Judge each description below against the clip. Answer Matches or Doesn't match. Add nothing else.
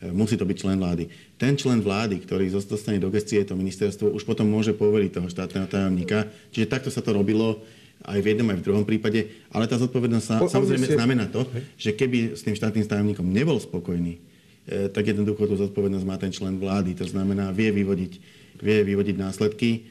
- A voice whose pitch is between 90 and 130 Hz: Matches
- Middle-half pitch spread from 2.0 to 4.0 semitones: Matches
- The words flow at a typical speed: Doesn't match